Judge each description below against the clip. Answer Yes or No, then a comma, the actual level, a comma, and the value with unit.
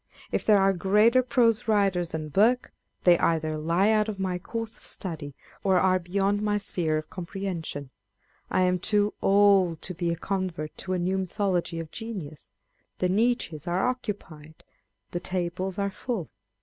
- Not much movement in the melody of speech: No, average, 3.2 semitones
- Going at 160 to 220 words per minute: Yes, average, 165 wpm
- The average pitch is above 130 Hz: Yes, medium, 185 Hz